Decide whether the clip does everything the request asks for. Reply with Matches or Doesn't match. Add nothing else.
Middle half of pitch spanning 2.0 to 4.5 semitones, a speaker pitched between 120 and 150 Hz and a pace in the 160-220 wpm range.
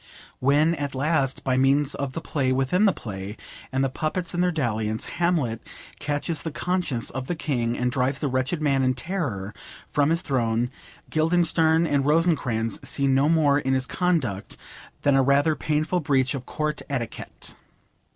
Matches